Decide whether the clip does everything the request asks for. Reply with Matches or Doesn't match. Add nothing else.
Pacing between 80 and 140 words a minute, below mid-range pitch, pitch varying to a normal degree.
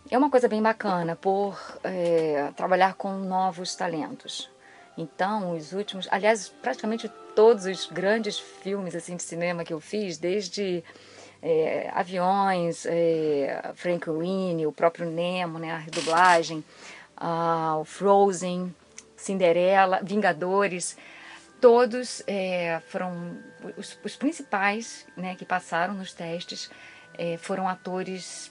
Doesn't match